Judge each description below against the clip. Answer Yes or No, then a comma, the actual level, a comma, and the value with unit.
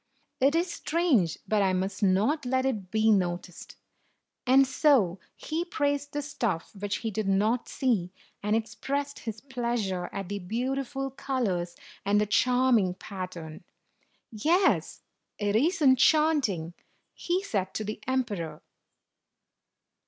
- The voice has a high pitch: Yes, high, 225 Hz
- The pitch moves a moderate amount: No, wide, 5.9 semitones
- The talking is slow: Yes, slow, 130 wpm